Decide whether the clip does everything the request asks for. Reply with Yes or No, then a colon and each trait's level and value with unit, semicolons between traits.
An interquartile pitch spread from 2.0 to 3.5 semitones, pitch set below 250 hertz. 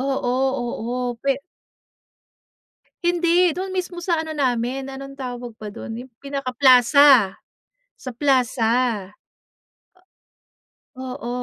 No: average, 2.9 semitones; very high, 265 Hz